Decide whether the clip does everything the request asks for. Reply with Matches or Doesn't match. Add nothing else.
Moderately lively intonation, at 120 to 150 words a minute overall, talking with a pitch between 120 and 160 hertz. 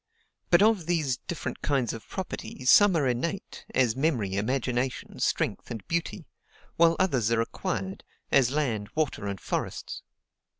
Doesn't match